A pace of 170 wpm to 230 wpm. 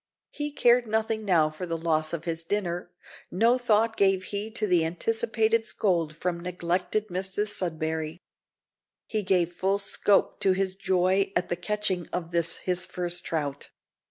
No: average, 155 wpm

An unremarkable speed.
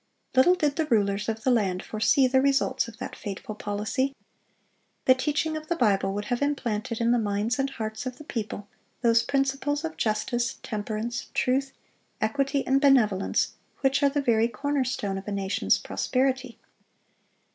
Yes: average, 170 wpm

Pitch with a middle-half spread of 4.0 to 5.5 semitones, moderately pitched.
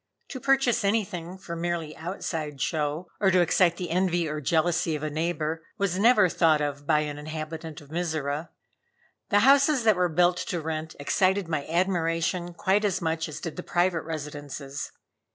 No: average, 3.0 semitones; medium, 165 Hz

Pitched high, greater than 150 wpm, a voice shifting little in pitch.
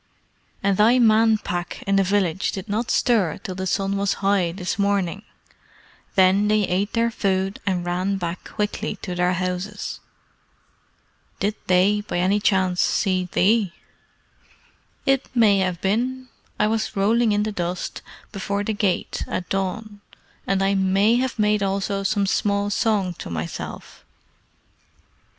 No: high, 200 Hz; average, 145 wpm; narrow, 2.3 semitones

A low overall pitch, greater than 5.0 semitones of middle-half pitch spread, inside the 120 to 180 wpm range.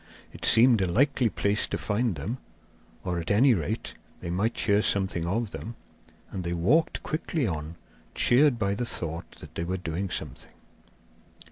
Yes: low, 100 Hz; wide, 5.6 semitones; average, 165 wpm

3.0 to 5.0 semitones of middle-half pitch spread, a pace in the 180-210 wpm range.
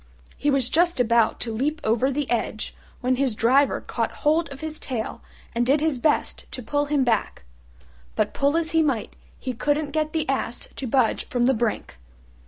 Yes: average, 3.8 semitones; average, 190 wpm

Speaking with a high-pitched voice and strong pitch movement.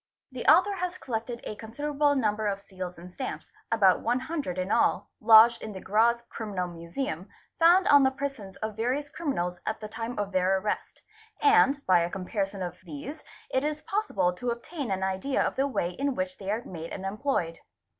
Yes: high, 220 Hz; wide, 6.6 semitones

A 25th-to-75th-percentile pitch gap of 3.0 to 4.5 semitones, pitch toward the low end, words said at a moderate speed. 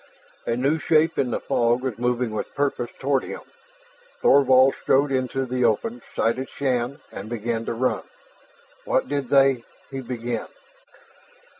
No: narrow, 2.4 semitones; low, 130 Hz; average, 150 wpm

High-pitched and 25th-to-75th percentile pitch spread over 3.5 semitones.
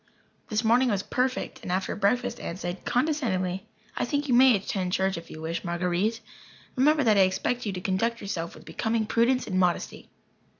Yes: high, 205 Hz; average, 4.8 semitones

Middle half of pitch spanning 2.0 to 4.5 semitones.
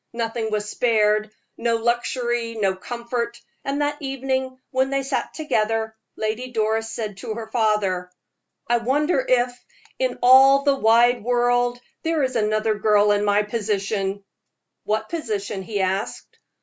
Yes: average, 3.1 semitones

